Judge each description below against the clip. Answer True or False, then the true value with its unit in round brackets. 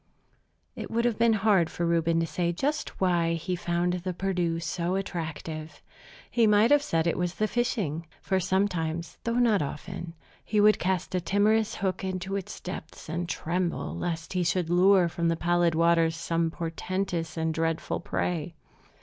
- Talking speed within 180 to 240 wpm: False (170 wpm)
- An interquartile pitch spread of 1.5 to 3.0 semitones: True (2.7 semitones)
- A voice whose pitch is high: False (175 Hz)